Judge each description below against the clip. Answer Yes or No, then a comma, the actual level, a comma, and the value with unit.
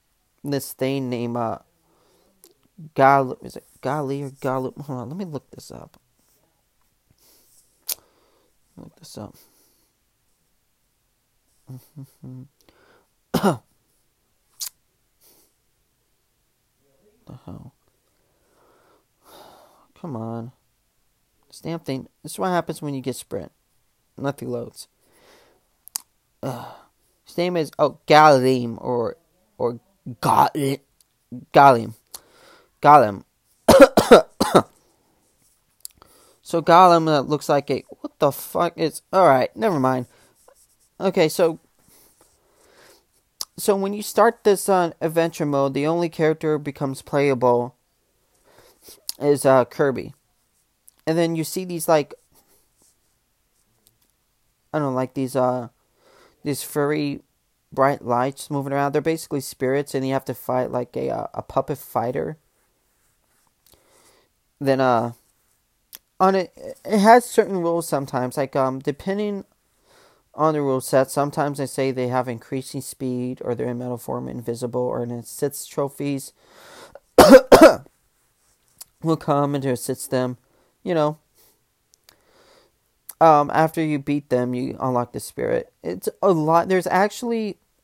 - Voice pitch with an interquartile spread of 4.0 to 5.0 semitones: Yes, average, 4.5 semitones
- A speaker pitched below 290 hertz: Yes, medium, 140 Hz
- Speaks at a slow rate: Yes, slow, 115 wpm